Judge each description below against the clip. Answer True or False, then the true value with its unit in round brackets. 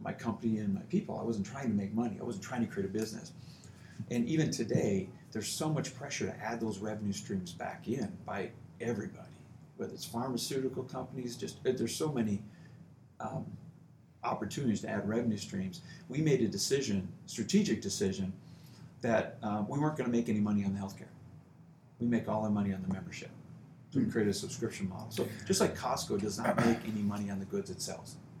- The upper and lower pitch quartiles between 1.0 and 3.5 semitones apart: True (2.8 semitones)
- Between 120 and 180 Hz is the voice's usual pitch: False (110 Hz)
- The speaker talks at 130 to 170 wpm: False (195 wpm)